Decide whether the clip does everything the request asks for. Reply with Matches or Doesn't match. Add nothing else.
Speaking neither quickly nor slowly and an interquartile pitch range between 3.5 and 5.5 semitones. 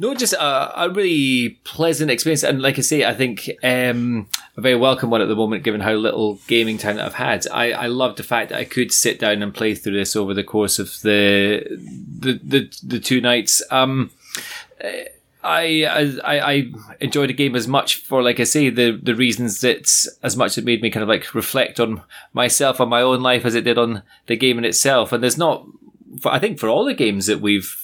Doesn't match